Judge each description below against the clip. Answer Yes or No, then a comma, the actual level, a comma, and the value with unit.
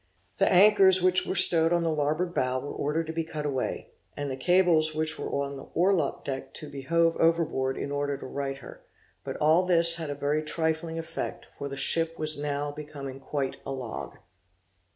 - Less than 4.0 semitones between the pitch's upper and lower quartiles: Yes, average, 2.9 semitones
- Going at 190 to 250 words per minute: Yes, average, 200 wpm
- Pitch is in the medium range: Yes, medium, 155 Hz